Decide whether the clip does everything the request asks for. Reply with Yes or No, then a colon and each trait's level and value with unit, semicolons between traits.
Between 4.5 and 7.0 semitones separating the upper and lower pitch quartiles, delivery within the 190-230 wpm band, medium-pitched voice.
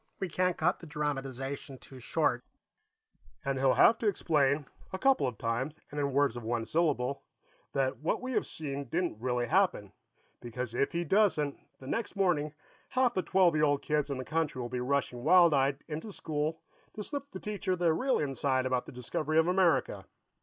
Yes: average, 5.1 semitones; average, 195 wpm; medium, 150 Hz